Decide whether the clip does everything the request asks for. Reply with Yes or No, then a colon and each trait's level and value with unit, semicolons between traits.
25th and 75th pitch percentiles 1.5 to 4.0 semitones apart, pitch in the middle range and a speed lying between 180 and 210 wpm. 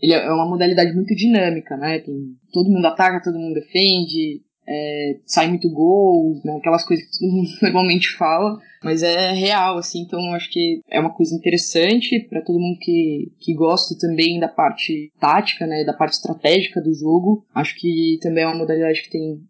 Yes: narrow, 2.5 semitones; medium, 170 Hz; fast, 185 wpm